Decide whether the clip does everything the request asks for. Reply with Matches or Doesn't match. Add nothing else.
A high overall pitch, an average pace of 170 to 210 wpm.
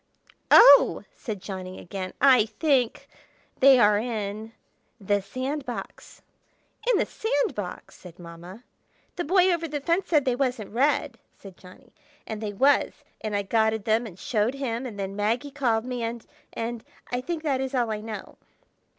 Doesn't match